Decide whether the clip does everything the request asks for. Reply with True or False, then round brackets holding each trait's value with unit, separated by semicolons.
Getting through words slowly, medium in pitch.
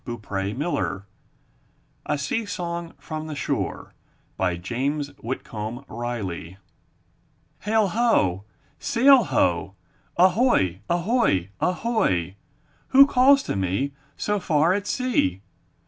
True (105 wpm; 150 Hz)